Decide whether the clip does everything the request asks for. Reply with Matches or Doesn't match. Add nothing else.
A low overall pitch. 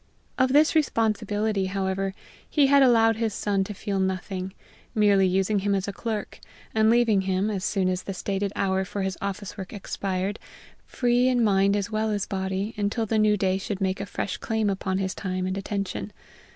Doesn't match